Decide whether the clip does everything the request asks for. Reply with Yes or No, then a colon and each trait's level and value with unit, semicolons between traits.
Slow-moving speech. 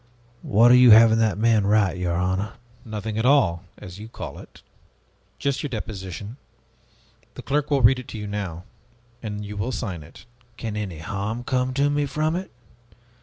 No: average, 180 wpm